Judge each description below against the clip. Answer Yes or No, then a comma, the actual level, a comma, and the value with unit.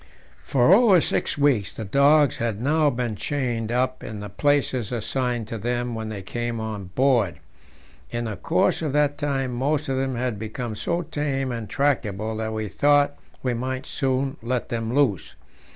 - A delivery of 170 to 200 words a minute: Yes, average, 175 wpm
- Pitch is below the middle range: Yes, low, 125 Hz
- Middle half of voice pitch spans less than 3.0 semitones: No, average, 4.1 semitones